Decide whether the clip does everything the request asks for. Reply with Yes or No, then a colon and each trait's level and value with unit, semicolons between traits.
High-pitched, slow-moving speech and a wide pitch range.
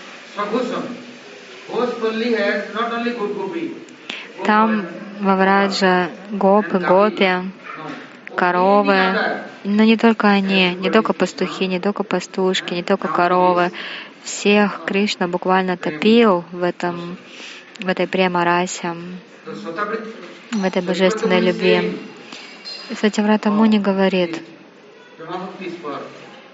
No: high, 195 Hz; slow, 75 wpm; average, 2.8 semitones